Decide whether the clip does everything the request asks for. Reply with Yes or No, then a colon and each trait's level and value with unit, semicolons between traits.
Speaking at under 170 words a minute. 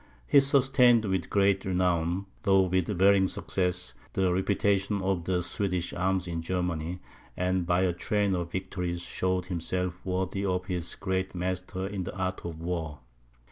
Yes: average, 155 wpm